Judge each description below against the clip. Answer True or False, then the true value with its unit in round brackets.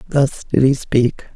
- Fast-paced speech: False (175 wpm)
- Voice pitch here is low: True (130 Hz)